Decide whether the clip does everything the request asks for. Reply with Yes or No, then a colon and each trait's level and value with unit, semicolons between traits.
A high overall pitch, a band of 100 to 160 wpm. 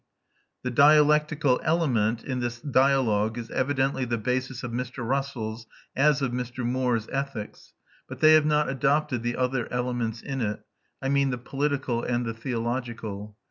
No: low, 125 Hz; average, 155 wpm